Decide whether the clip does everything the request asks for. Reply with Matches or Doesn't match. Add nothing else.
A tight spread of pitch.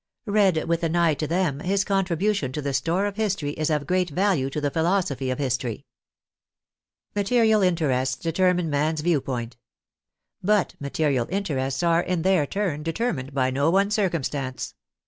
Doesn't match